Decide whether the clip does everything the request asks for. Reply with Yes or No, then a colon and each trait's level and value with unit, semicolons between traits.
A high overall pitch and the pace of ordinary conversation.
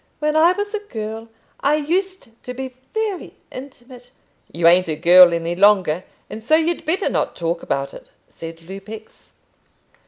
Yes: high, 225 Hz; average, 165 wpm